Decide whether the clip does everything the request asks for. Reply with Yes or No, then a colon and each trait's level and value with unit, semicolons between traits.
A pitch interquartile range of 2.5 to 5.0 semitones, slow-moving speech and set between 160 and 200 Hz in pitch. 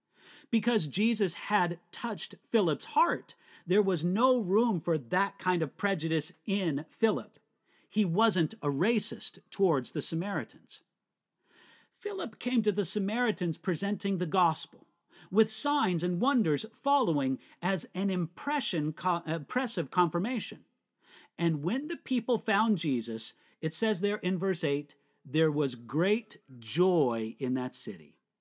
No: wide, 5.4 semitones; slow, 130 wpm; high, 190 Hz